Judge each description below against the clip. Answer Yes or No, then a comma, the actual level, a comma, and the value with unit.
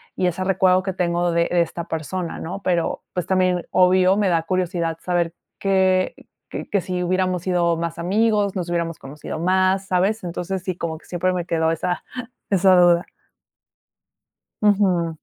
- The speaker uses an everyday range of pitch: No, narrow, 1.7 semitones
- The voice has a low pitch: No, medium, 180 Hz